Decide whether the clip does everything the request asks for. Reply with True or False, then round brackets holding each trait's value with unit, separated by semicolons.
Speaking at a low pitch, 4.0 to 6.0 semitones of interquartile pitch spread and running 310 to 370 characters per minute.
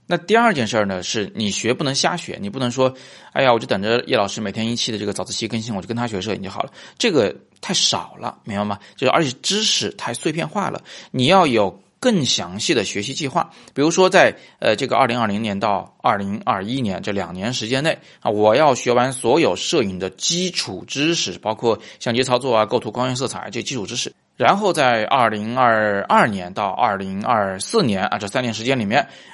True (120 Hz; 4.5 semitones; 320 characters per minute)